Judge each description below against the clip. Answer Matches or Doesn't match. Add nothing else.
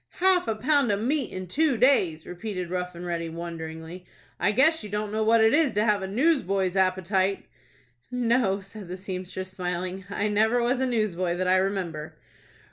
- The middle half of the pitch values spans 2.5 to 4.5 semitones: Matches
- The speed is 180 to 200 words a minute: Matches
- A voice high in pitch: Matches